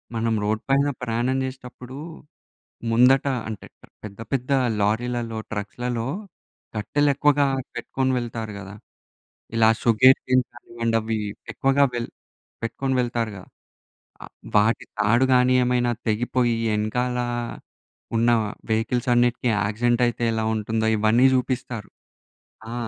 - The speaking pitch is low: Yes, low, 120 Hz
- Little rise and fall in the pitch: Yes, narrow, 2.3 semitones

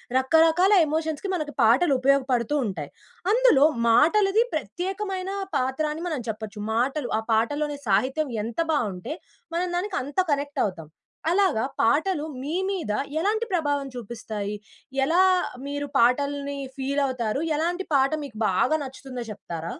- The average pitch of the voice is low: No, very high, 285 Hz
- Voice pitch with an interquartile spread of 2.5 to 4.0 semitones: No, wide, 5.6 semitones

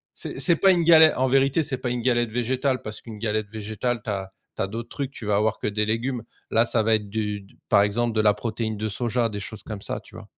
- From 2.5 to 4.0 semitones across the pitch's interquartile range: Yes, average, 2.9 semitones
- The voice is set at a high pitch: No, low, 110 Hz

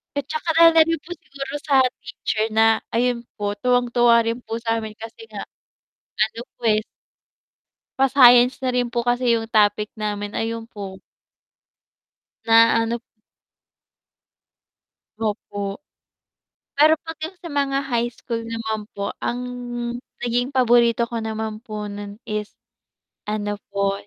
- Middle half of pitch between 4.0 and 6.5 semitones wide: No, average, 2.8 semitones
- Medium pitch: No, high, 230 Hz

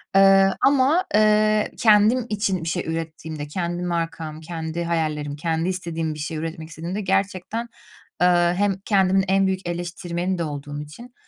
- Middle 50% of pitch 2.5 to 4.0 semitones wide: Yes, average, 3.3 semitones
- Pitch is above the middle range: No, medium, 175 Hz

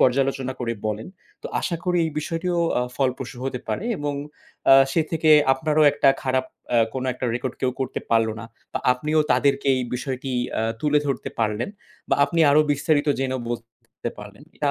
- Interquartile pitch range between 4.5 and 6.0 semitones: No, average, 3.0 semitones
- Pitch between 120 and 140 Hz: Yes, low, 135 Hz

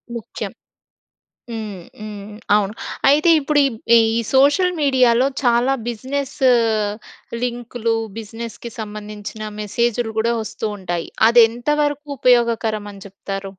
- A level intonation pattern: No, average, 3.3 semitones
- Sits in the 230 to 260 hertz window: Yes, high, 235 Hz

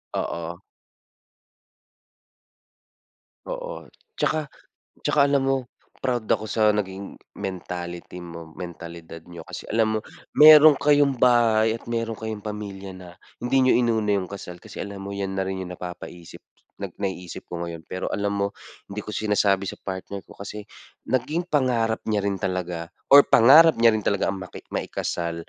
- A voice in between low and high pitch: No, low, 100 Hz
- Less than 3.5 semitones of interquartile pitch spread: No, average, 4.1 semitones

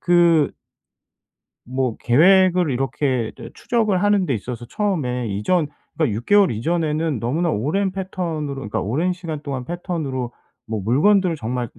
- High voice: No, medium, 150 Hz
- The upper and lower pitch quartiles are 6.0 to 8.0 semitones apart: Yes, wide, 6.5 semitones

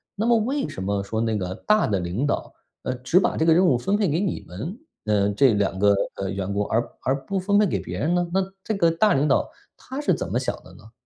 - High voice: No, medium, 140 Hz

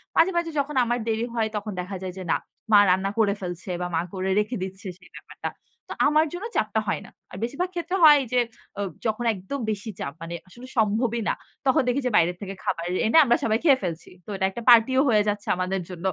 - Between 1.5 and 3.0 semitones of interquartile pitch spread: No, average, 4.8 semitones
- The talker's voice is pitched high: Yes, high, 215 Hz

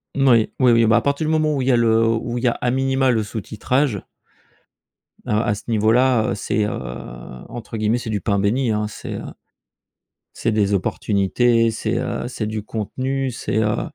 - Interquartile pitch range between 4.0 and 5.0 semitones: No, average, 3.0 semitones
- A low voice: Yes, low, 115 Hz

